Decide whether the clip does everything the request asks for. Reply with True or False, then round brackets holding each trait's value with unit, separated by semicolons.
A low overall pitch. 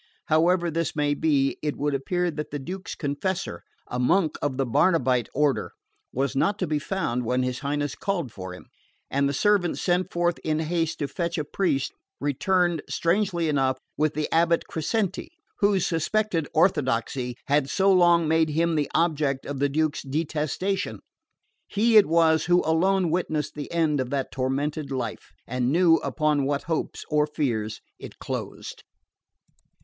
False (155 Hz)